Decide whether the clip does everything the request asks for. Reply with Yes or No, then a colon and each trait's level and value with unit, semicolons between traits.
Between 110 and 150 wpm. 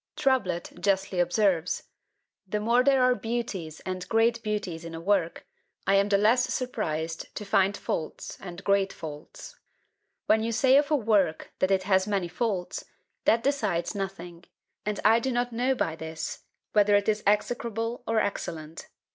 No: average, 165 wpm